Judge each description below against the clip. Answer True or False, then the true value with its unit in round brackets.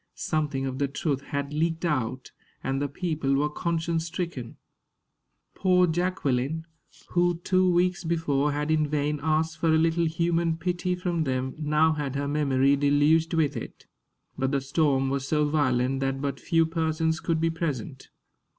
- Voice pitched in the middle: True (155 Hz)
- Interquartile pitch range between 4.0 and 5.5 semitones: False (3.0 semitones)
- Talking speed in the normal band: True (160 wpm)